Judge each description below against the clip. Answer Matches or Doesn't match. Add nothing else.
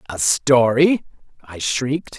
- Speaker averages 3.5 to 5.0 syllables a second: Matches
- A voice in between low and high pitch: Doesn't match